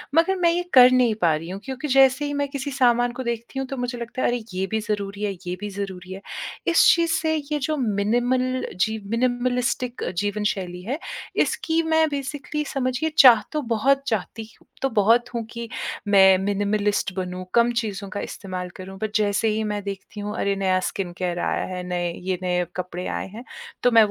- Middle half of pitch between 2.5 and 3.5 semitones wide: No, average, 4.7 semitones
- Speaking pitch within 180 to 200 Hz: No, high, 225 Hz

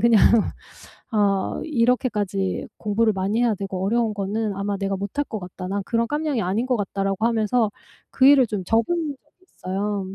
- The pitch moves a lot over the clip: No, average, 3.3 semitones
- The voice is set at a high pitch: Yes, high, 210 Hz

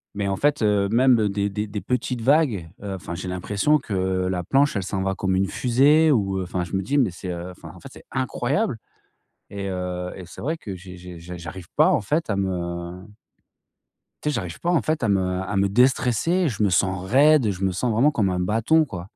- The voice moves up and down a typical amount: No, wide, 5.7 semitones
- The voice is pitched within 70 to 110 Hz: Yes, low, 100 Hz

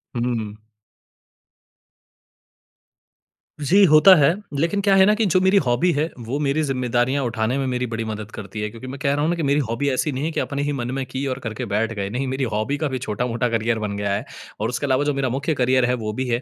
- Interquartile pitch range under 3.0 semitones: No, average, 3.9 semitones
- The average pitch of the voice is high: No, low, 130 Hz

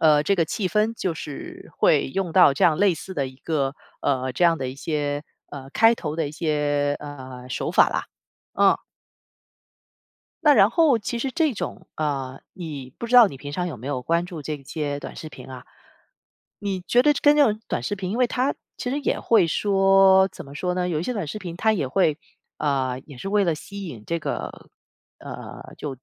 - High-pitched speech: No, medium, 165 Hz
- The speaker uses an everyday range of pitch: No, wide, 5.8 semitones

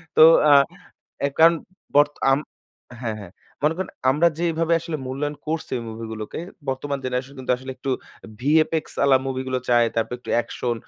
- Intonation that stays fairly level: No, average, 4.0 semitones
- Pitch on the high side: No, low, 135 Hz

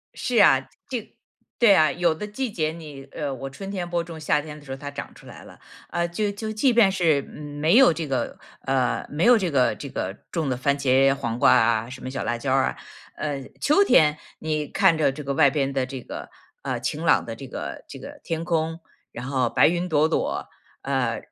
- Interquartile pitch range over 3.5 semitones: Yes, average, 4.3 semitones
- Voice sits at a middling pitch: Yes, medium, 150 Hz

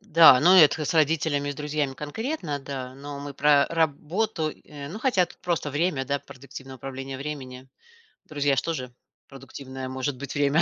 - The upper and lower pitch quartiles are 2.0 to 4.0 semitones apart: Yes, average, 2.8 semitones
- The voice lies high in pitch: No, medium, 145 Hz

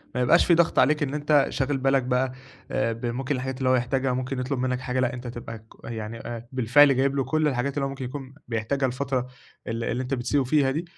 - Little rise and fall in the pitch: Yes, narrow, 1.9 semitones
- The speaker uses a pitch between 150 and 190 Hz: No, low, 130 Hz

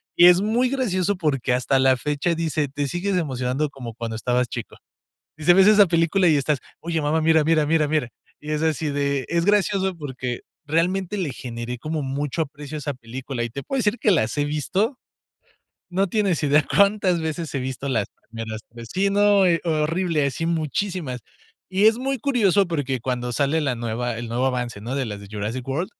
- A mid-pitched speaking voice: Yes, medium, 150 Hz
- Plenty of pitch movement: Yes, wide, 5.8 semitones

